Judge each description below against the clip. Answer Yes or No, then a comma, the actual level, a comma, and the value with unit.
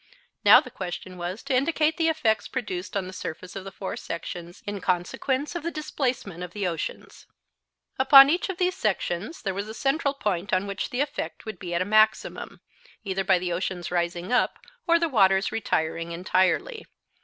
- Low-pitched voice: No, high, 200 Hz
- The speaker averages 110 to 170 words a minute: No, average, 190 wpm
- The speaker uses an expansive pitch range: Yes, wide, 7.1 semitones